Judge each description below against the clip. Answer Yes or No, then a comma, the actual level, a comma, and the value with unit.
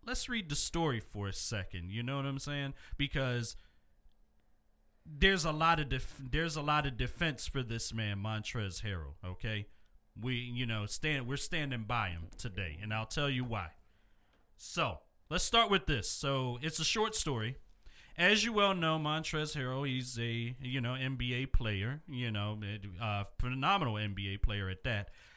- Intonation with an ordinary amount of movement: No, wide, 5.8 semitones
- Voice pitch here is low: Yes, low, 125 Hz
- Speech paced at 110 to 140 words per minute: No, average, 175 wpm